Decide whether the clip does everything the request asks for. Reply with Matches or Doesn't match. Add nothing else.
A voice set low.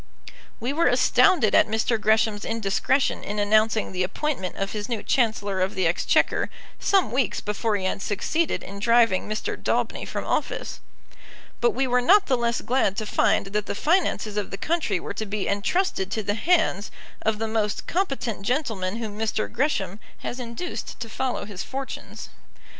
Doesn't match